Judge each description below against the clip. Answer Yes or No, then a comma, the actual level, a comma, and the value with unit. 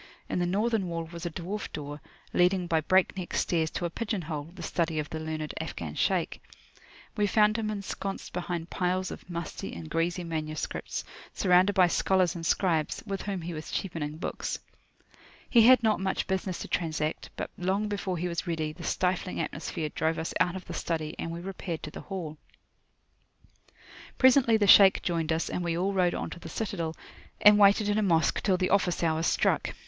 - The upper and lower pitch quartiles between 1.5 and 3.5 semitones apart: Yes, average, 3.1 semitones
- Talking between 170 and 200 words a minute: Yes, average, 195 wpm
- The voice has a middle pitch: Yes, medium, 175 Hz